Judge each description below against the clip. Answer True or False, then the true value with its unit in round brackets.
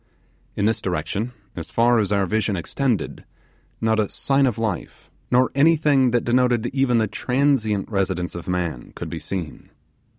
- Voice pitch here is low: True (110 Hz)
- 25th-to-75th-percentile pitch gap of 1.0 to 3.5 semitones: False (4.6 semitones)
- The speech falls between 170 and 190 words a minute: False (160 wpm)